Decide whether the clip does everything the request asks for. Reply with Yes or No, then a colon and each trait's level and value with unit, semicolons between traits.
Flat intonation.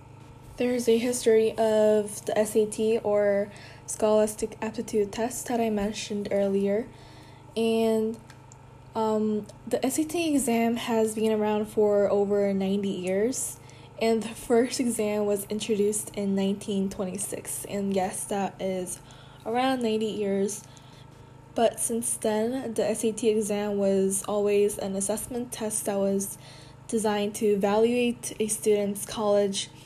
Yes: narrow, 2.2 semitones